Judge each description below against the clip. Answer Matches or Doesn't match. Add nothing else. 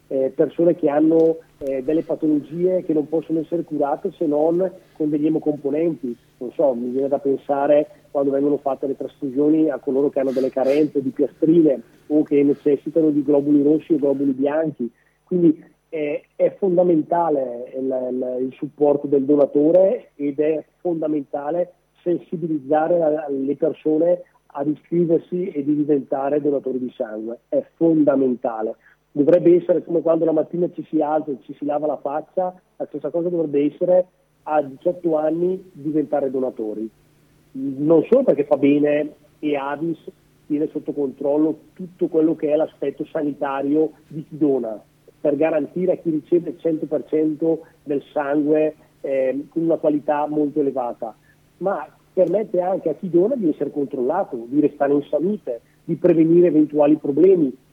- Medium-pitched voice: Matches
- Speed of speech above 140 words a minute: Matches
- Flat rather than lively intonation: Matches